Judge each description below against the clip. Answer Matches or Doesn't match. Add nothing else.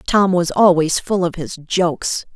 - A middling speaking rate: Matches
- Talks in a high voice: Doesn't match